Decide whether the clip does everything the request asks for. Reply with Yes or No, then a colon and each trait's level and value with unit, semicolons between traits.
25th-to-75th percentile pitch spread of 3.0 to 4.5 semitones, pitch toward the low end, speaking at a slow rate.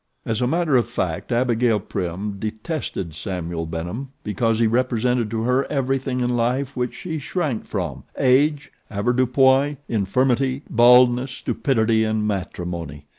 Yes: average, 3.7 semitones; low, 120 Hz; slow, 130 wpm